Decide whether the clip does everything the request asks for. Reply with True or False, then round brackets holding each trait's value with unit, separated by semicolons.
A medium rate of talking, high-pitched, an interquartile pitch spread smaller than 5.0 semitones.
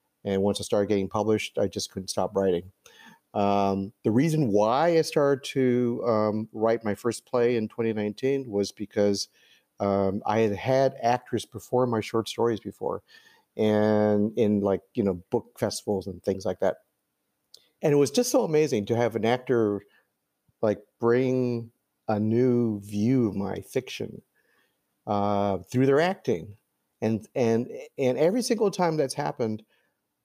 False (155 wpm; 110 Hz; 3.7 semitones)